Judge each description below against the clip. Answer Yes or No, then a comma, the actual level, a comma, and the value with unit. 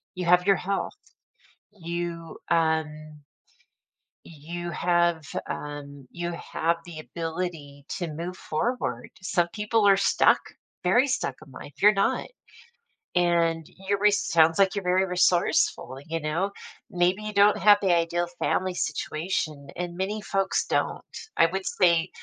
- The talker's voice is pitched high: No, medium, 175 Hz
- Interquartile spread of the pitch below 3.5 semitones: Yes, average, 2.9 semitones